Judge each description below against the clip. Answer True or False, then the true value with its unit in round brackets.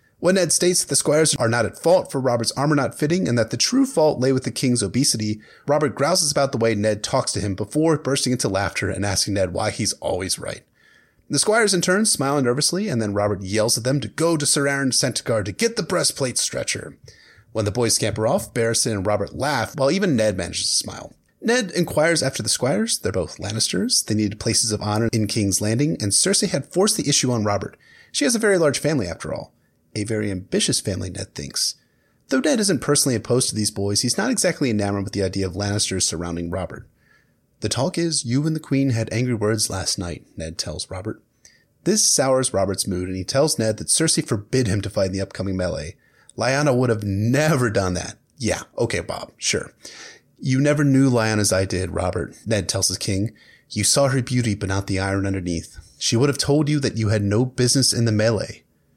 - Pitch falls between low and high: False (115 Hz)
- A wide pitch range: True (5.9 semitones)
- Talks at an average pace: False (220 wpm)